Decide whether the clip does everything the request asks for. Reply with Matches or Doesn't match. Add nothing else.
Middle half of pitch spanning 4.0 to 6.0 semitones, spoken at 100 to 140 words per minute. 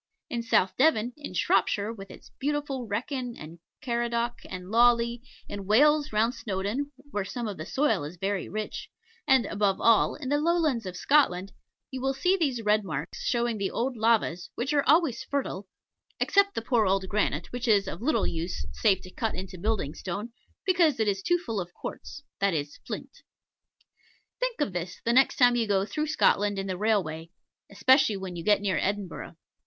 Doesn't match